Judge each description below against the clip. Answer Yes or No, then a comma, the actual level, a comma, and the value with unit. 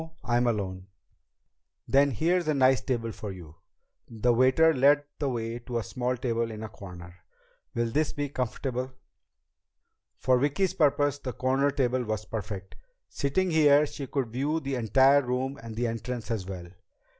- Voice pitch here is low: Yes, low, 125 Hz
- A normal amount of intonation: Yes, average, 3.7 semitones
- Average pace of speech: Yes, average, 160 wpm